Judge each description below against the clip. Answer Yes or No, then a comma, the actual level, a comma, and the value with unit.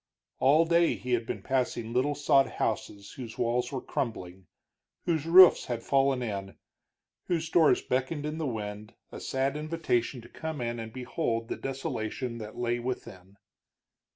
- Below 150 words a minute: No, average, 155 wpm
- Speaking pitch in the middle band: No, low, 125 Hz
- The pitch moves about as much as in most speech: Yes, average, 4.0 semitones